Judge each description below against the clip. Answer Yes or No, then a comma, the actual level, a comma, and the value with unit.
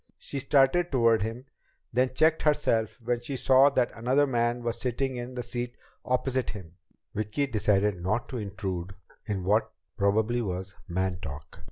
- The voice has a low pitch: Yes, low, 120 Hz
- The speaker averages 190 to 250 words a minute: No, average, 160 wpm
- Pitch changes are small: No, average, 4.4 semitones